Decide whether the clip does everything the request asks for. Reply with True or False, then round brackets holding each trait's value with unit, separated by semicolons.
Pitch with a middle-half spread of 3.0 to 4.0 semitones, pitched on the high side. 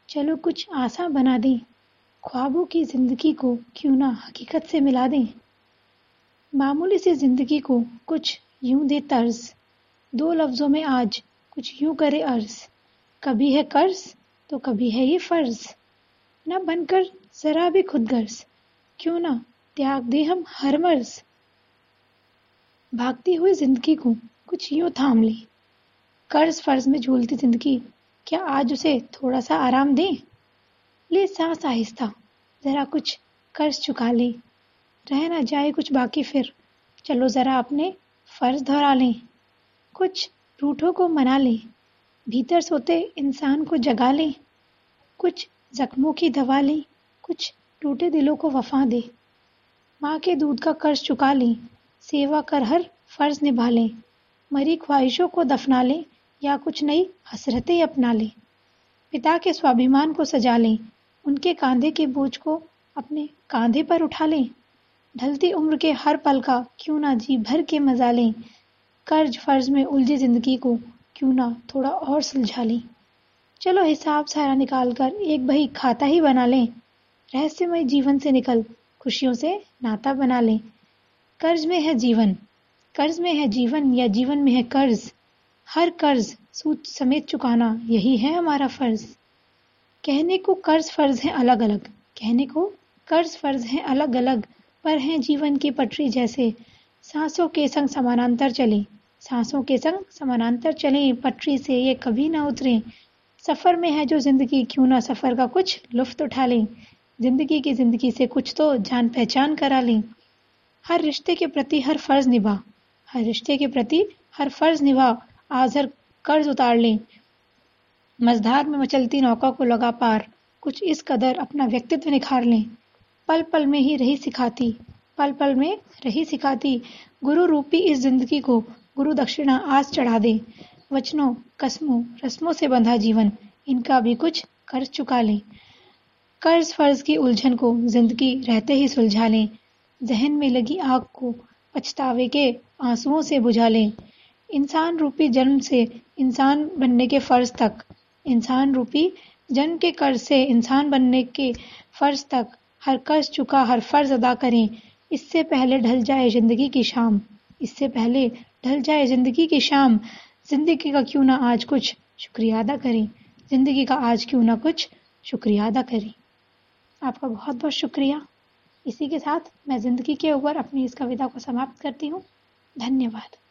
True (3.6 semitones; 270 Hz)